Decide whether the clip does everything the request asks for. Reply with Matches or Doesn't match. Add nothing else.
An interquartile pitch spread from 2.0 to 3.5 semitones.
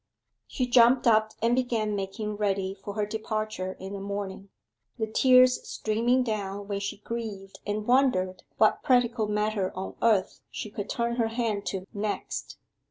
Matches